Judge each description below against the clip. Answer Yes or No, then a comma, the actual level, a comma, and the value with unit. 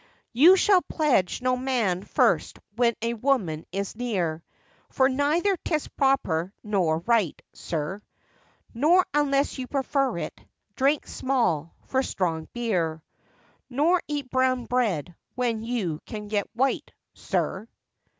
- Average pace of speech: No, slow, 125 wpm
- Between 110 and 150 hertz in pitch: No, high, 240 Hz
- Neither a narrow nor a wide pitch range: No, wide, 6.6 semitones